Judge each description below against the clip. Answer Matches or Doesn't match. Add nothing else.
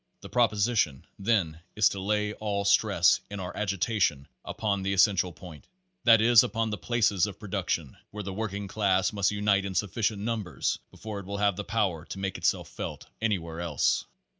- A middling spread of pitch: Doesn't match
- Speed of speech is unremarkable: Matches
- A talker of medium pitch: Doesn't match